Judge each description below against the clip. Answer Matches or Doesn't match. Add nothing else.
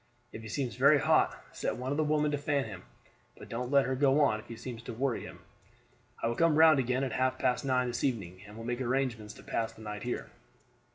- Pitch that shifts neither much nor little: Matches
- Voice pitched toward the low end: Matches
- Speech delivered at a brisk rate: Matches